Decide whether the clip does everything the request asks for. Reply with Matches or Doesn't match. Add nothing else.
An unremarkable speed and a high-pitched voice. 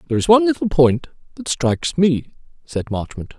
Doesn't match